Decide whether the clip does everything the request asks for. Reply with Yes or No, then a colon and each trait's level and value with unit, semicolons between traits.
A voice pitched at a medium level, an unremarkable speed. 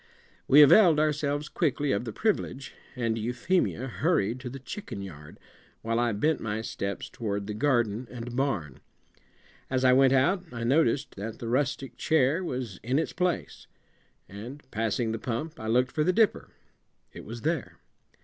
No: low, 125 Hz; average, 165 wpm